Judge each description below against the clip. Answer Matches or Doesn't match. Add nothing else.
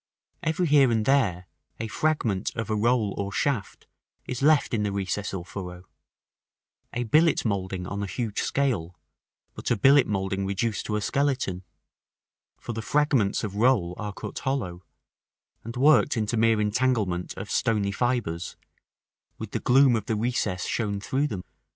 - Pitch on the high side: Doesn't match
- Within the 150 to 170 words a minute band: Matches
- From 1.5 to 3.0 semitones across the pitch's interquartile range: Doesn't match